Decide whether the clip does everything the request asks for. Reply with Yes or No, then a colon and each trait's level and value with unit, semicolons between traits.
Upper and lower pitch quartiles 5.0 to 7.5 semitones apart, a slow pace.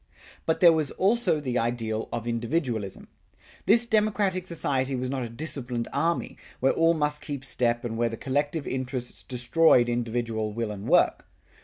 No: wide, 5.4 semitones; average, 160 wpm